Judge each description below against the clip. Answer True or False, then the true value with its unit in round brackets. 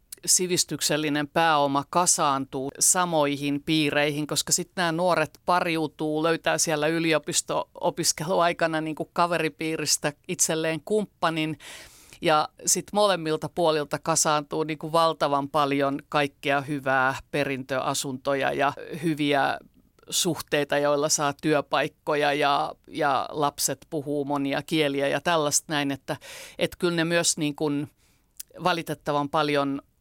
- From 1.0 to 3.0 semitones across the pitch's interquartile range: True (2.5 semitones)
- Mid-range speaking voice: True (155 Hz)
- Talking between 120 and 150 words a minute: False (100 wpm)